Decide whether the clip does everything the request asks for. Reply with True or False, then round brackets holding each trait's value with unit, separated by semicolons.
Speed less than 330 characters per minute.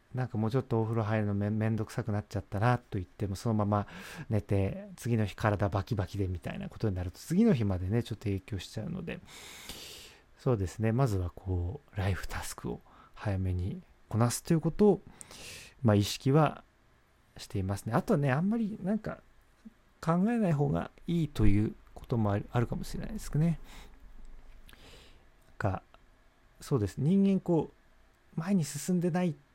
True (310 characters per minute)